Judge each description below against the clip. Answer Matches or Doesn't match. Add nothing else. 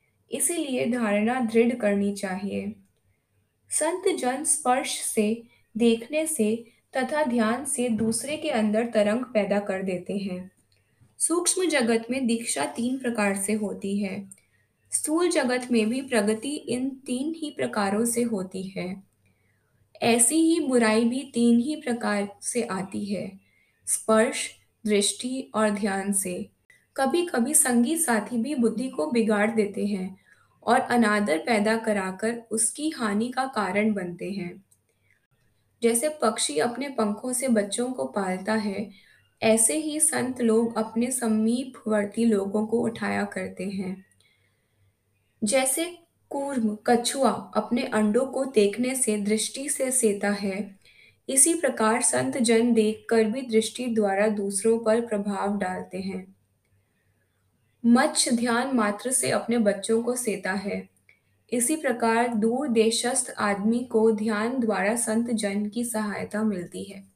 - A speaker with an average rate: Matches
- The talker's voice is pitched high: Matches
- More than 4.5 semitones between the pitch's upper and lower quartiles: Doesn't match